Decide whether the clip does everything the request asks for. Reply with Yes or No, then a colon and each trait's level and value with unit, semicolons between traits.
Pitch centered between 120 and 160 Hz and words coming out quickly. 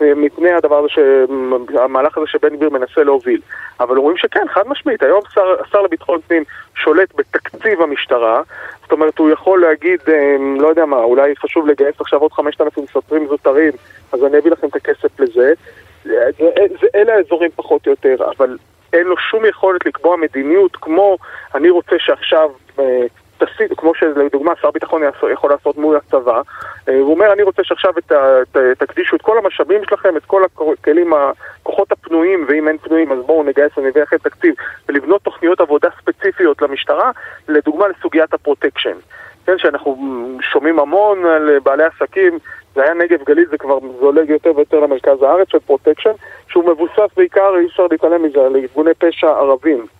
No: medium, 170 Hz; fast, 160 wpm